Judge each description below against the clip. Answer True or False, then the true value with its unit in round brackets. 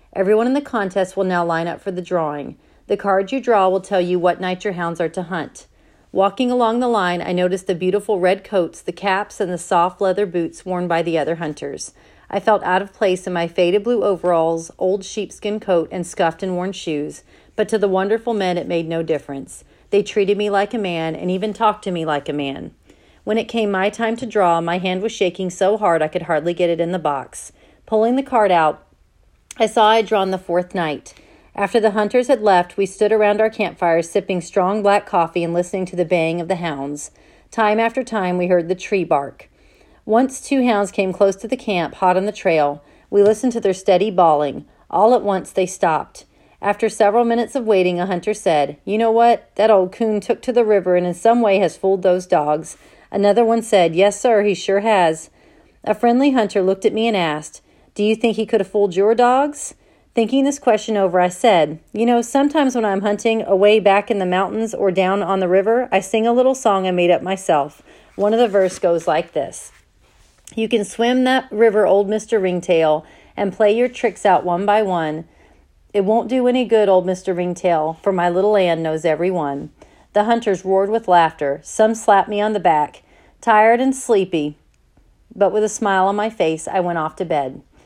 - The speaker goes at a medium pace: False (220 wpm)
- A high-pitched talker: True (195 Hz)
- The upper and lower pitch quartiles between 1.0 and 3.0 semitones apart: False (3.7 semitones)